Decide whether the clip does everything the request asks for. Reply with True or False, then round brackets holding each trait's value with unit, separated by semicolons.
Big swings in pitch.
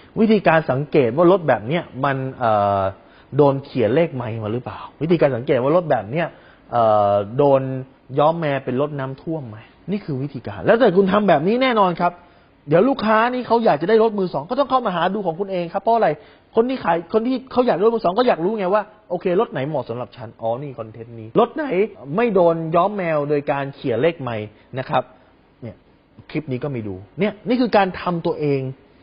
True (7.7 semitones)